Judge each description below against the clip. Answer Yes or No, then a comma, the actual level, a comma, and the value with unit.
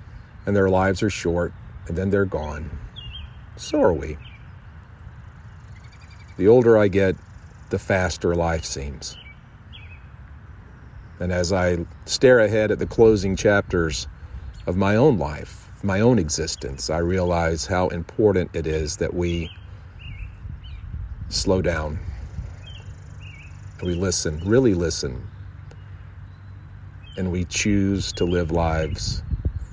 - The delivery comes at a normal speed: No, slow, 115 wpm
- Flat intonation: No, average, 3.0 semitones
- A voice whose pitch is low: Yes, very low, 95 Hz